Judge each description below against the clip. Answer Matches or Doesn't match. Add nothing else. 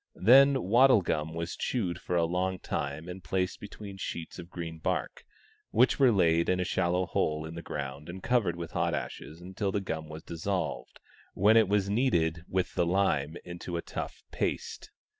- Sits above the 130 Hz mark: Doesn't match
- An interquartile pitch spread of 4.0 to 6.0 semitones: Doesn't match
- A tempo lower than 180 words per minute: Doesn't match